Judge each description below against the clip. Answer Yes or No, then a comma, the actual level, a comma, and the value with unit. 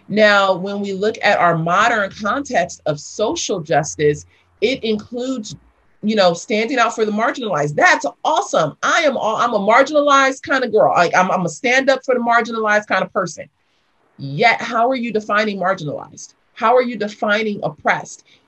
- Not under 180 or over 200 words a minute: No, average, 170 wpm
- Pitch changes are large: No, average, 4.6 semitones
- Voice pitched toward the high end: Yes, high, 210 Hz